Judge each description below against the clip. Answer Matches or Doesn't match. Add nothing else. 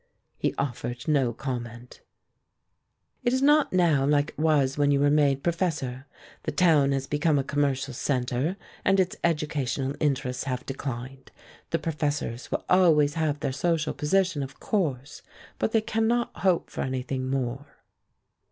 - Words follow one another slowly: Doesn't match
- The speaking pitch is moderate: Matches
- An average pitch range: Matches